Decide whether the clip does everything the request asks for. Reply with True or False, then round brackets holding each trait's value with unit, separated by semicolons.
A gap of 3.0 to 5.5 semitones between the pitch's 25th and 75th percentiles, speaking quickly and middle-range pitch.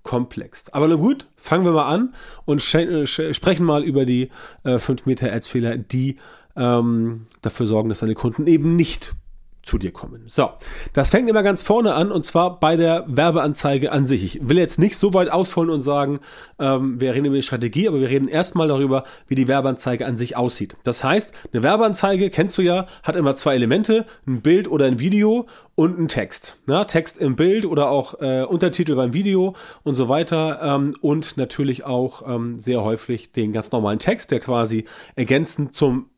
True (5.0 semitones; 195 wpm; 145 Hz)